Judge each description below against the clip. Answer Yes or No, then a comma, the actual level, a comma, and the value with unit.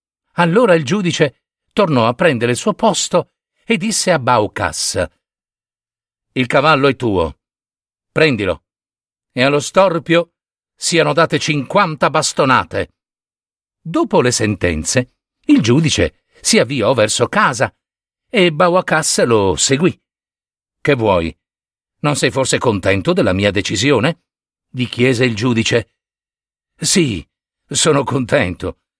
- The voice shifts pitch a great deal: Yes, wide, 7.2 semitones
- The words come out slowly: Yes, slow, 110 wpm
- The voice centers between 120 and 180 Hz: Yes, medium, 140 Hz